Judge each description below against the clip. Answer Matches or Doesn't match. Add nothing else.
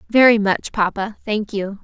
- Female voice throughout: Matches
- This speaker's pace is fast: Doesn't match